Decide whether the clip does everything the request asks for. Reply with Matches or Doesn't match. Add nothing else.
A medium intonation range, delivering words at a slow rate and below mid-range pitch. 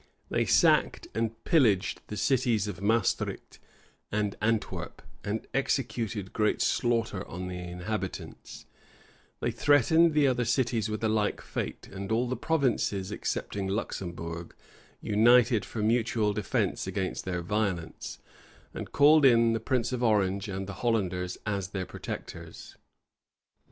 Matches